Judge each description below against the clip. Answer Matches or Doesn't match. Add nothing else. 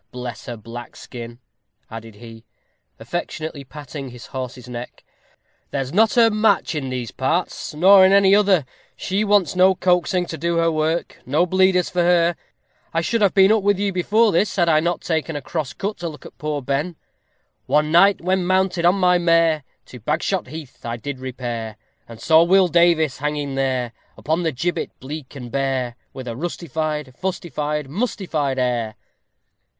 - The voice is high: Doesn't match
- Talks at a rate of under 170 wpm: Doesn't match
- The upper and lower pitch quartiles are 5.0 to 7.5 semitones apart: Matches